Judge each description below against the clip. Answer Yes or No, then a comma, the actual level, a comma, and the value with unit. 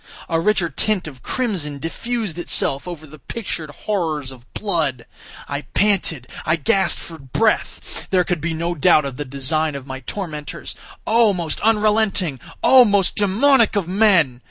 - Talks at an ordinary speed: Yes, average, 155 wpm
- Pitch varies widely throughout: Yes, wide, 5.9 semitones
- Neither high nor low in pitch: Yes, medium, 170 Hz